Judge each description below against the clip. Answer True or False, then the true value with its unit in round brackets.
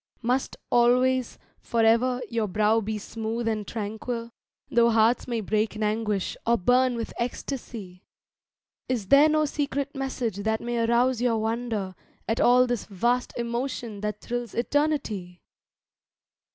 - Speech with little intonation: True (2.3 semitones)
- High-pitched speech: True (235 Hz)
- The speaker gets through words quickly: False (135 wpm)